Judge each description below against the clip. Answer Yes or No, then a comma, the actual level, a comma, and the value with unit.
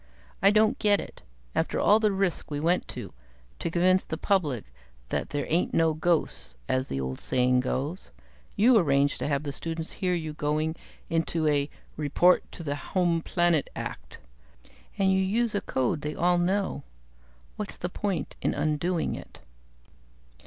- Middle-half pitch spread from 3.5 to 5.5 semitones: Yes, average, 4.3 semitones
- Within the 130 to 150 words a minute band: No, average, 160 wpm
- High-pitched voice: No, medium, 165 Hz